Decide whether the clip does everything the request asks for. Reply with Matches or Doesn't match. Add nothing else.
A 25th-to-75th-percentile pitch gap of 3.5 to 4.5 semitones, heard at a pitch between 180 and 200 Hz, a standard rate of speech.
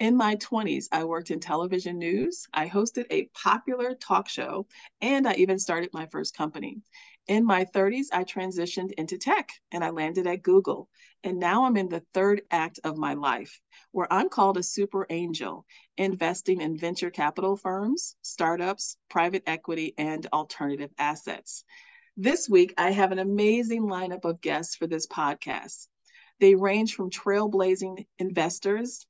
Matches